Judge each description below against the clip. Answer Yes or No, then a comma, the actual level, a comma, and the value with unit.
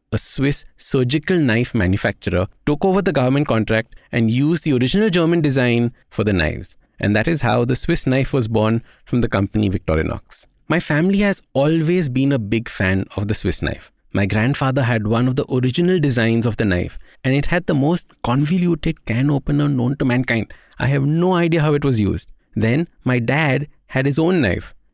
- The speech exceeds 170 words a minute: Yes, average, 195 wpm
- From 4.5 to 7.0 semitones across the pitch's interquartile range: Yes, wide, 5.5 semitones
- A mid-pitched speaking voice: No, low, 130 Hz